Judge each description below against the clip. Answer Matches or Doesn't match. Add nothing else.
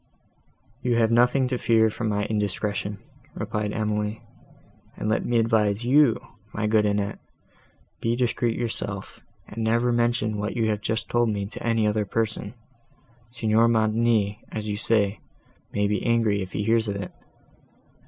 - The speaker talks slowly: Doesn't match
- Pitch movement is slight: Matches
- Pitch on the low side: Matches